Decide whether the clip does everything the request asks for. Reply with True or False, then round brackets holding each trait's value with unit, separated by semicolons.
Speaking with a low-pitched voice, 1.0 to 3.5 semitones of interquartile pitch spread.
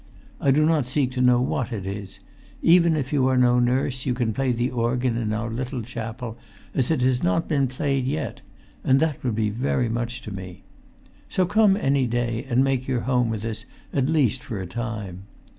True (125 Hz; 2.8 semitones)